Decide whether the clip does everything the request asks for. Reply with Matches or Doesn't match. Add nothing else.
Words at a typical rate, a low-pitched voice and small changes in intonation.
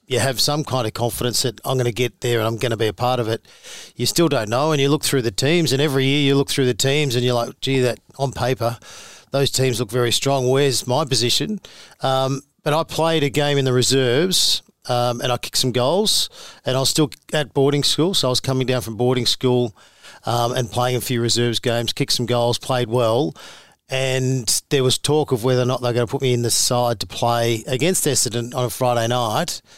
Doesn't match